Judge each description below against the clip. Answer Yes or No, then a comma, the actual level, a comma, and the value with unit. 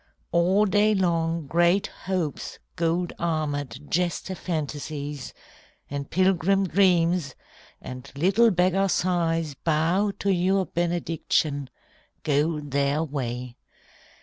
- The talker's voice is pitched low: No, medium, 165 Hz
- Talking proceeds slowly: Yes, slow, 95 wpm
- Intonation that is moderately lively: Yes, average, 4.0 semitones